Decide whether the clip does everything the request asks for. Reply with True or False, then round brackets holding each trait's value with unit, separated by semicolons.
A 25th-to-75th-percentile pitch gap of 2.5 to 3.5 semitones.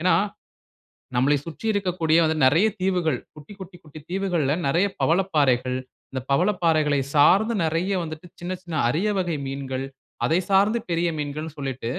False (4.2 semitones)